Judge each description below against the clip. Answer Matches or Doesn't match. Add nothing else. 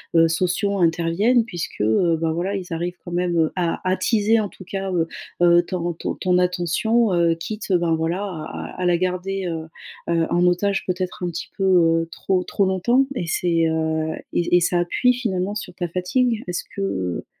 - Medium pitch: Matches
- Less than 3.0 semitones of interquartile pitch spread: Matches